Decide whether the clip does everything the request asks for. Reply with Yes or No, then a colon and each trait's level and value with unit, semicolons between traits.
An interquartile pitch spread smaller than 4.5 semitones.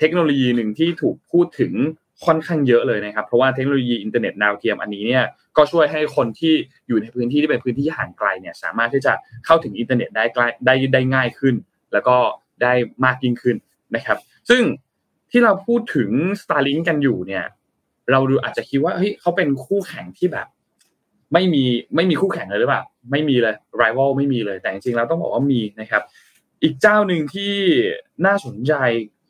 No: wide, 5.5 semitones